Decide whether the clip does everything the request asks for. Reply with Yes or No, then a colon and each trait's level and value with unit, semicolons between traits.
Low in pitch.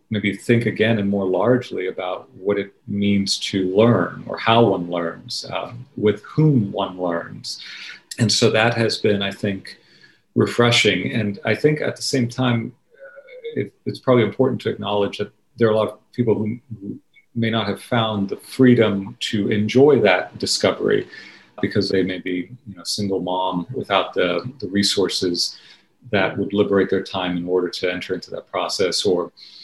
Yes: low, 105 Hz